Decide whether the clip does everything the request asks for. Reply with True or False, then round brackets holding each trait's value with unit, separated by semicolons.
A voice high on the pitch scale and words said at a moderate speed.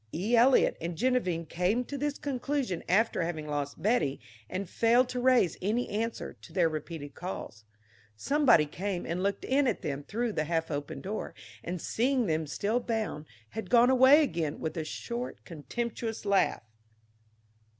True (200 Hz; 160 wpm)